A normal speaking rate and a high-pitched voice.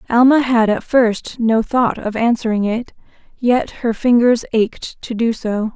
Yes: average, 165 wpm; high, 230 Hz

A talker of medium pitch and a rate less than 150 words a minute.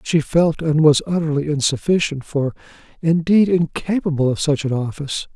Yes: medium, 155 Hz; slow, 135 wpm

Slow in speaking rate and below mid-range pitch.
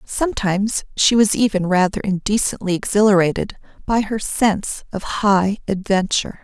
No: slow, 120 wpm; high, 200 Hz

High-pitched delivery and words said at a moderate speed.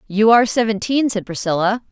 Yes: high, 215 Hz; average, 155 wpm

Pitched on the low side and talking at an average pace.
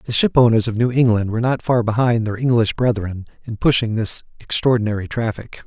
Yes: low, 115 Hz; average, 190 wpm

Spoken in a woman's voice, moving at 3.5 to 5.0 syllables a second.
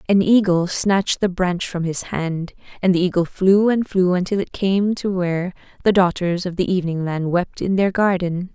Yes: female; 4.9 syllables/s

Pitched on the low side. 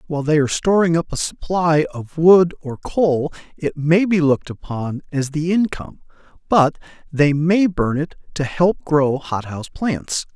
No: medium, 155 Hz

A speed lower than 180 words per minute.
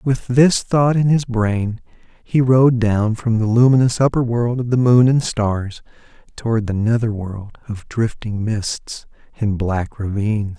Yes: average, 165 wpm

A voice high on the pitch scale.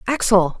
Yes: high, 210 Hz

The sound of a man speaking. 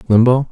Yes: male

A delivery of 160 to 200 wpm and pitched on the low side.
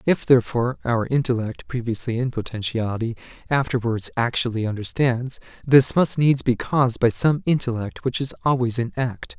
No: average, 145 wpm; low, 125 Hz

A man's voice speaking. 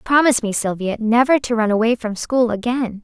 No: female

